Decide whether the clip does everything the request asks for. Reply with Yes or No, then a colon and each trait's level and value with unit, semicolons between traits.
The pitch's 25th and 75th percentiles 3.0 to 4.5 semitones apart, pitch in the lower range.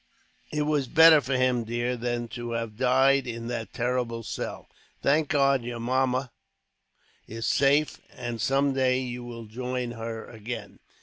No: narrow, 2.5 semitones; low, 125 Hz